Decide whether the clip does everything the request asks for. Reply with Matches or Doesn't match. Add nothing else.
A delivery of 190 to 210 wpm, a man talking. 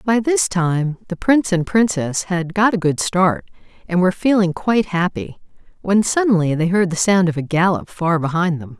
Doesn't match